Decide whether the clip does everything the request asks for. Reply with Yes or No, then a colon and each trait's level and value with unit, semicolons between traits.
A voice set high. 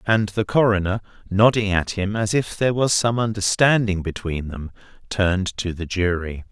No: low, 100 Hz